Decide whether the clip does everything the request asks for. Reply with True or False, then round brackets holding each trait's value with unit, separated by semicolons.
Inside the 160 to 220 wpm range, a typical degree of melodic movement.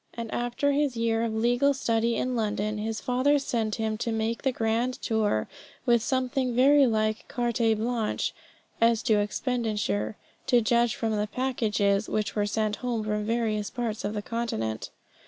False (165 wpm; 2.2 semitones)